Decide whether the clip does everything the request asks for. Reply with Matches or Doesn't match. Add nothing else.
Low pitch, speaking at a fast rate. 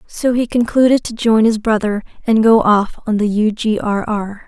Doesn't match